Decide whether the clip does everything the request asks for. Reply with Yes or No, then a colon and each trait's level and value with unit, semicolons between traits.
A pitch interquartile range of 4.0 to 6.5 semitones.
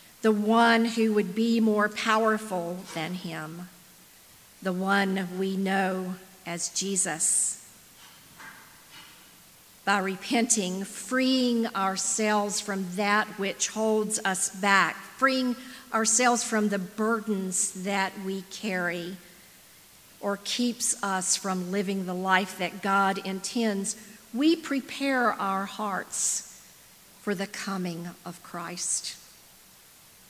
No: narrow, 2.6 semitones